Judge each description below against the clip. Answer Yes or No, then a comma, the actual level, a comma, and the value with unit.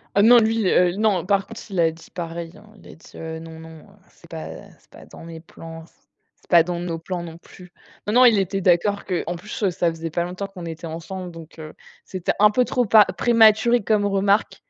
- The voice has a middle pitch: Yes, medium, 180 Hz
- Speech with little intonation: No, average, 3.8 semitones